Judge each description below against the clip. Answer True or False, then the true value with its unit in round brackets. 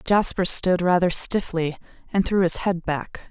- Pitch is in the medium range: True (180 Hz)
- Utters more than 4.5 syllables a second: False (4.1 syllables/s)